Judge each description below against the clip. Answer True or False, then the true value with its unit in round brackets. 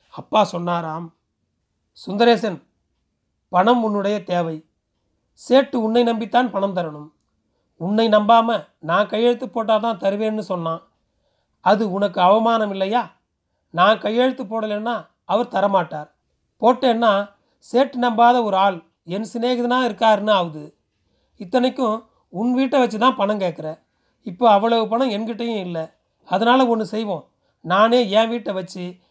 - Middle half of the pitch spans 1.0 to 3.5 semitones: False (5.0 semitones)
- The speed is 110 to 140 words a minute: True (115 wpm)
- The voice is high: True (215 Hz)